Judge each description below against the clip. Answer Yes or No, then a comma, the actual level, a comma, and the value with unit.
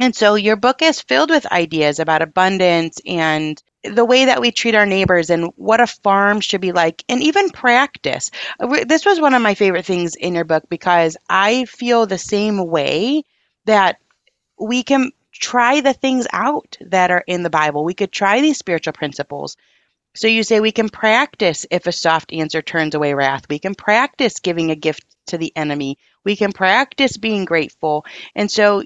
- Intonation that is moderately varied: No, wide, 6.3 semitones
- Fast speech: No, average, 190 wpm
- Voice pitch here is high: Yes, high, 195 Hz